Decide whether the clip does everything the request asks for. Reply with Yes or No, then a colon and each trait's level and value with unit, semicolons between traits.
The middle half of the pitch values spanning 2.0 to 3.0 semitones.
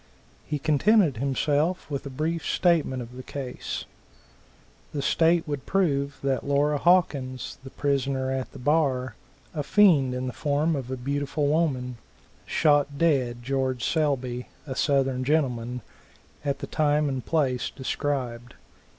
Yes: average, 2.7 semitones